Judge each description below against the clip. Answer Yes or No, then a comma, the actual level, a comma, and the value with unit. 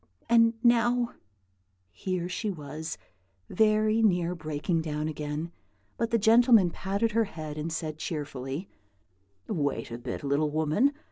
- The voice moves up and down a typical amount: No, wide, 6.4 semitones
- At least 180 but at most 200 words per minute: No, slow, 135 wpm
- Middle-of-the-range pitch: Yes, medium, 170 Hz